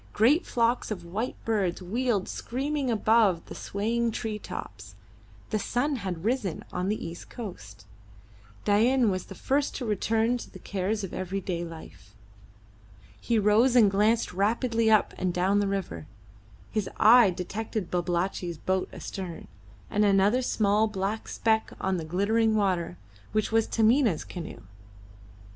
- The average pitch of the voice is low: No, high, 210 Hz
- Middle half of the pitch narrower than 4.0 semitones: Yes, average, 3.6 semitones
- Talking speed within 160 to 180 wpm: No, average, 145 wpm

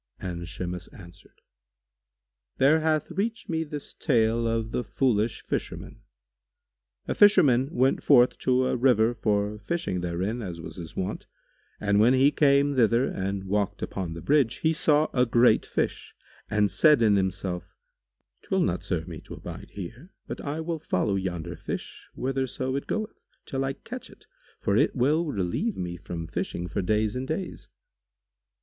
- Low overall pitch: Yes, low, 115 Hz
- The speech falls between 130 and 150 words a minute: No, average, 160 wpm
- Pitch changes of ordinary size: No, wide, 7.0 semitones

